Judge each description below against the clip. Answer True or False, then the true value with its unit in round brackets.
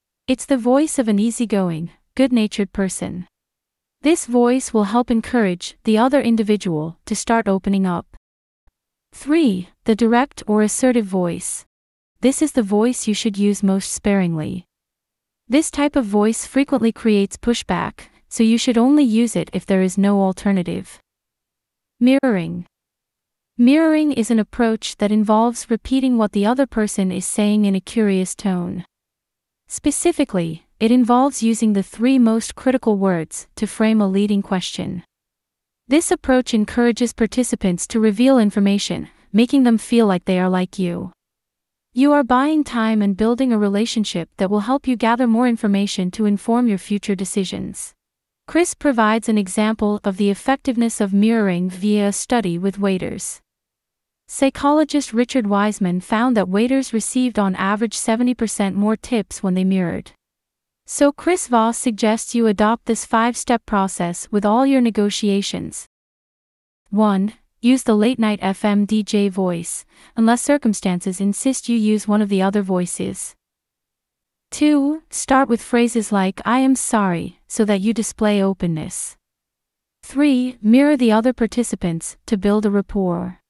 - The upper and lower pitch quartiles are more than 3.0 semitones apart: True (3.8 semitones)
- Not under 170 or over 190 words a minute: False (145 wpm)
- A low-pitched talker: False (220 Hz)